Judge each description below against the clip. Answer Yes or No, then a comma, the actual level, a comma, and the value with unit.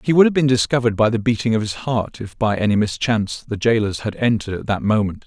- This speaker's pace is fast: Yes, fast, 250 wpm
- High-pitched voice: No, low, 110 Hz